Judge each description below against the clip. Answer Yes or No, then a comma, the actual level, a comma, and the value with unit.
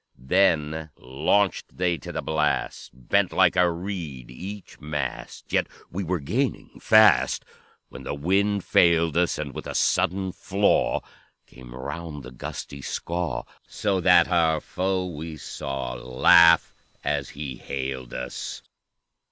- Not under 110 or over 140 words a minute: Yes, slow, 135 wpm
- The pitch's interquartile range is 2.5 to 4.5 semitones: No, average, 5.0 semitones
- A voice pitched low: Yes, very low, 85 Hz